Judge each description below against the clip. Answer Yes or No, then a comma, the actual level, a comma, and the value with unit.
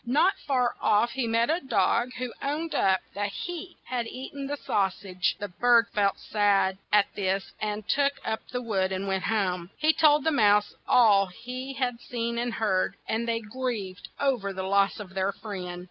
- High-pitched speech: Yes, high, 220 Hz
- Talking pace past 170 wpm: Yes, average, 195 wpm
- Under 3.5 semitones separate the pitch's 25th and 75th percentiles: No, average, 4.3 semitones